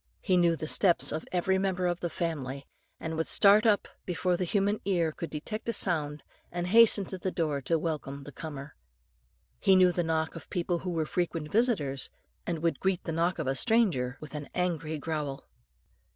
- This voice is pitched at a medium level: Yes, medium, 170 Hz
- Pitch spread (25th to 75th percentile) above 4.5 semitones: No, average, 3.4 semitones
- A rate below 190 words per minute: No, average, 195 wpm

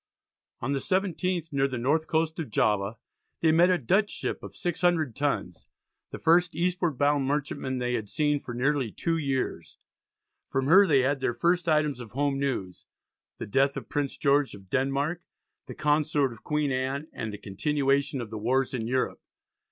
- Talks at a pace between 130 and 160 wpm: No, average, 180 wpm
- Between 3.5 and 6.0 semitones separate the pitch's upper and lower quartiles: Yes, average, 3.8 semitones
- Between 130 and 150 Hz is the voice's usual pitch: Yes, medium, 140 Hz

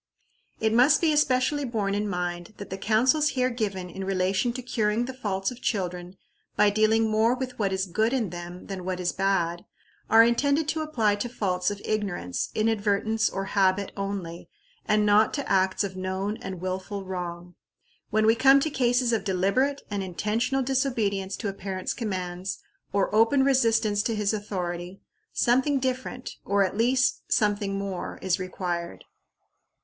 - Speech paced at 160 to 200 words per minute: Yes, average, 165 wpm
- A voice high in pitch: Yes, high, 205 Hz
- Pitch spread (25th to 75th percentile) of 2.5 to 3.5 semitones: No, average, 4.1 semitones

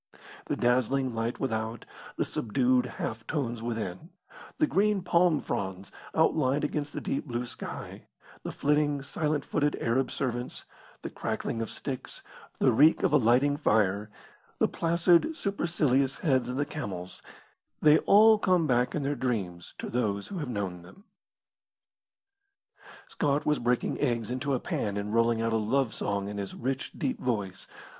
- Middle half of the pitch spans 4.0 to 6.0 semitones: Yes, average, 4.8 semitones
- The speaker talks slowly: No, average, 155 wpm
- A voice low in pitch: Yes, low, 125 Hz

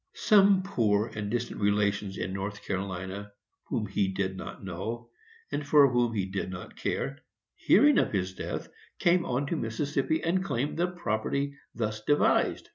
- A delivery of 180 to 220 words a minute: No, average, 160 wpm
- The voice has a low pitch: Yes, low, 110 Hz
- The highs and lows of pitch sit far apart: Yes, wide, 6.4 semitones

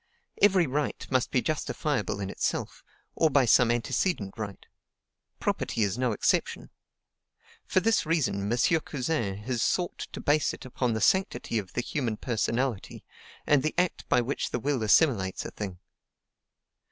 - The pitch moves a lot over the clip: Yes, wide, 5.9 semitones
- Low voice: Yes, low, 125 Hz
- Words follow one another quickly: No, average, 155 wpm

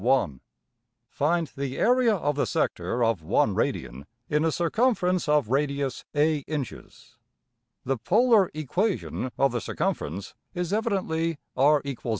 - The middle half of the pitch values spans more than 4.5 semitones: Yes, average, 5.1 semitones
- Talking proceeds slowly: Yes, slow, 120 wpm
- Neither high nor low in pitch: Yes, medium, 150 Hz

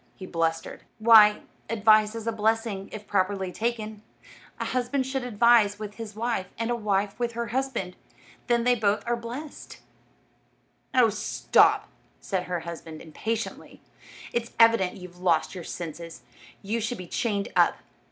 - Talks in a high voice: Yes, high, 215 Hz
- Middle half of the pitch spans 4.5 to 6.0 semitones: No, average, 3.5 semitones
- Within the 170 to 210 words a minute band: No, average, 150 wpm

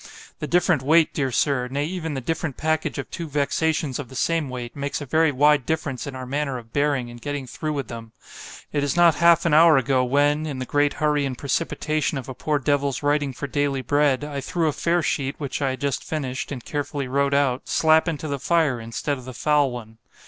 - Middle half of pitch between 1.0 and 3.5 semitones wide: Yes, average, 2.7 semitones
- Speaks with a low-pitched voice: No, medium, 145 Hz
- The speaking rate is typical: No, fast, 220 wpm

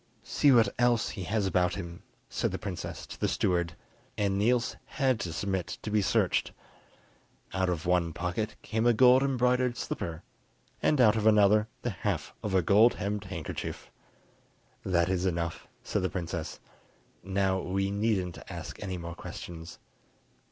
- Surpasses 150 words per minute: Yes, average, 160 wpm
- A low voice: Yes, very low, 95 Hz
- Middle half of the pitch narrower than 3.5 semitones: No, average, 3.8 semitones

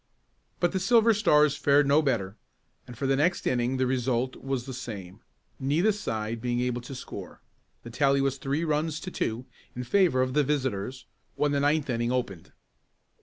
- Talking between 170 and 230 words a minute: Yes, average, 180 wpm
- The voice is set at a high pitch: No, low, 135 Hz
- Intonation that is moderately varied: Yes, average, 3.5 semitones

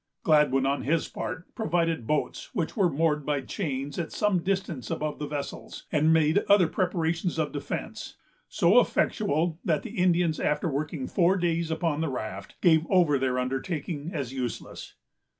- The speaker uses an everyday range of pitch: Yes, average, 3.2 semitones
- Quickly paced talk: No, average, 160 wpm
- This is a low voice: No, medium, 160 Hz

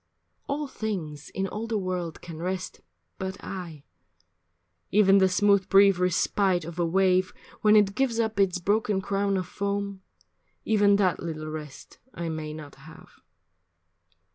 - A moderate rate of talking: Yes, average, 145 wpm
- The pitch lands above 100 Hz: Yes, high, 190 Hz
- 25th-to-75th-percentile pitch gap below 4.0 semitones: Yes, average, 2.9 semitones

